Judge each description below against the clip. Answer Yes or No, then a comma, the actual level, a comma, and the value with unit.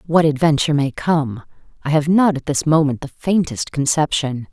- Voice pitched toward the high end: No, medium, 150 Hz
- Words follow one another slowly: No, average, 175 wpm